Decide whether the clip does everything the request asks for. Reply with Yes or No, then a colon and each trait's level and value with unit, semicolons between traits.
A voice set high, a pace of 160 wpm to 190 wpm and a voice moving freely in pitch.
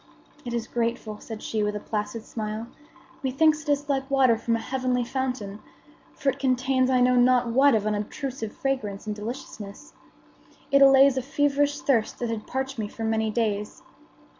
No: high, 245 Hz; average, 175 wpm; average, 3.6 semitones